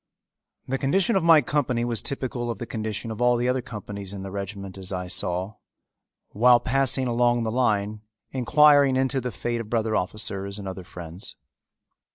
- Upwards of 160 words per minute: Yes, average, 180 wpm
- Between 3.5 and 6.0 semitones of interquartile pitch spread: Yes, average, 4.4 semitones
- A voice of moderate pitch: No, low, 115 Hz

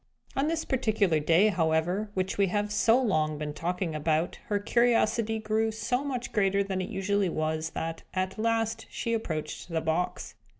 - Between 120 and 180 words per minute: Yes, average, 170 wpm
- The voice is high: Yes, high, 200 Hz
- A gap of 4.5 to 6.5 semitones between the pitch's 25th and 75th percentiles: Yes, average, 5.3 semitones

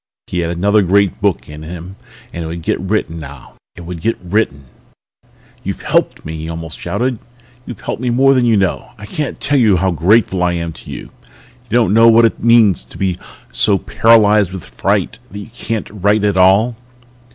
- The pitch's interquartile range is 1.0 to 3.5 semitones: No, average, 4.6 semitones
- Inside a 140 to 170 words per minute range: No, average, 200 wpm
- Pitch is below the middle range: Yes, low, 100 Hz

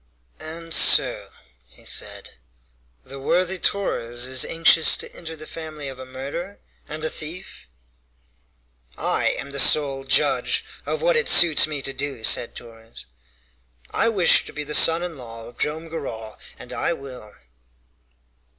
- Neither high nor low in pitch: Yes, medium, 150 Hz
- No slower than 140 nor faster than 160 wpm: Yes, average, 150 wpm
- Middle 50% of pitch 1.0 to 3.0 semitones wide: No, average, 4.2 semitones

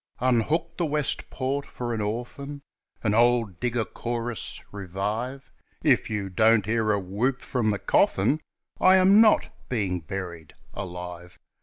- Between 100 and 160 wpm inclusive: Yes, average, 140 wpm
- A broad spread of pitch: No, average, 4.8 semitones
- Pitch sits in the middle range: No, low, 115 Hz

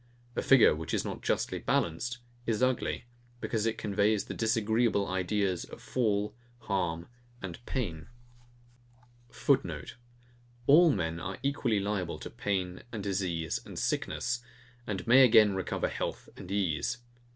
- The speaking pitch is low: Yes, low, 105 Hz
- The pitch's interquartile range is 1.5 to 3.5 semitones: No, average, 4.1 semitones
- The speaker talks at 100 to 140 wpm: Yes, slow, 135 wpm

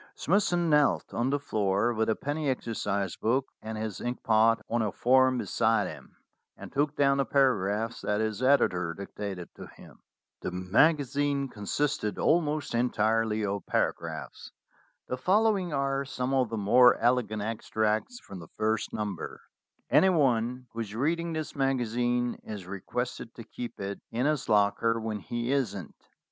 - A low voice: Yes, low, 120 Hz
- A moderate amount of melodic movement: Yes, average, 4.4 semitones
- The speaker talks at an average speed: Yes, average, 155 wpm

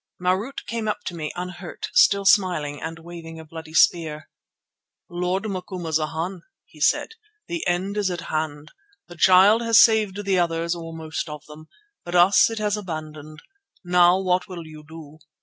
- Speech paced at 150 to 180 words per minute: Yes, average, 165 wpm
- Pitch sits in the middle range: Yes, medium, 175 Hz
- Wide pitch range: No, average, 3.2 semitones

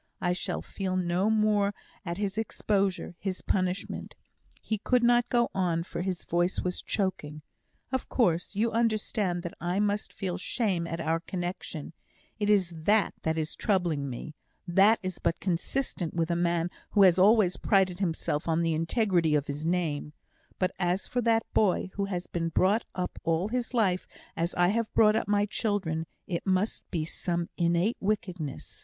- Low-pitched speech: No, medium, 185 Hz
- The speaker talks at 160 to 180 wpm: Yes, average, 175 wpm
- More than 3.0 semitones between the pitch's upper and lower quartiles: Yes, average, 3.4 semitones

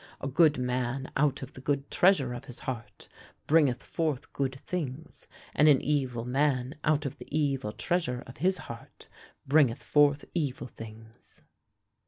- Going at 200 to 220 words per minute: No, average, 155 wpm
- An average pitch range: Yes, average, 3.1 semitones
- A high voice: No, low, 135 Hz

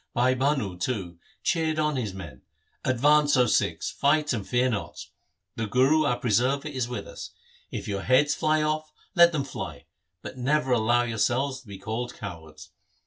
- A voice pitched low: Yes, low, 125 Hz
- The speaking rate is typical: Yes, average, 175 wpm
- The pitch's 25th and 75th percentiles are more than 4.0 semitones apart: Yes, average, 5.0 semitones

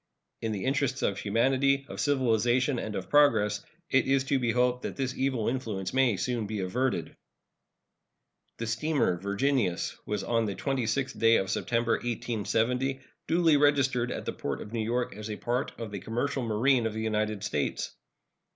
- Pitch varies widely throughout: No, average, 3.7 semitones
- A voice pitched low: Yes, low, 120 Hz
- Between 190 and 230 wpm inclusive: No, average, 170 wpm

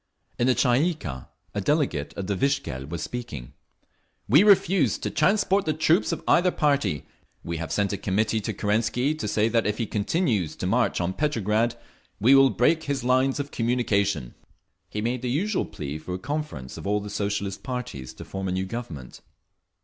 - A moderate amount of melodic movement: No, wide, 6.5 semitones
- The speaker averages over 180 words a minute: Yes, average, 190 wpm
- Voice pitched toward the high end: No, low, 115 Hz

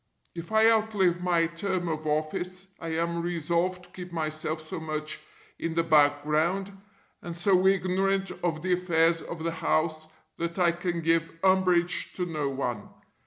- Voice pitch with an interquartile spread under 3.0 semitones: Yes, narrow, 2.4 semitones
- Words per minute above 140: Yes, average, 160 wpm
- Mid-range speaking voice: Yes, medium, 170 Hz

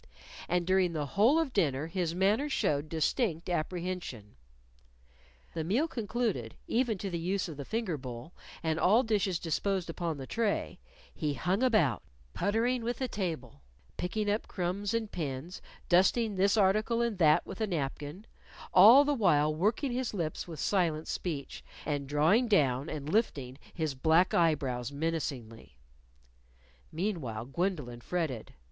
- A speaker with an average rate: Yes, average, 150 wpm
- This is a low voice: No, medium, 175 Hz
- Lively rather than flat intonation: Yes, wide, 6.0 semitones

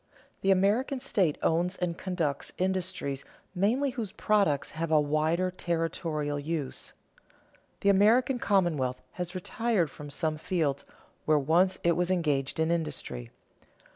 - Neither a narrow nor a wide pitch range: Yes, average, 3.9 semitones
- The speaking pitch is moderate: Yes, medium, 170 Hz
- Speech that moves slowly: Yes, slow, 130 wpm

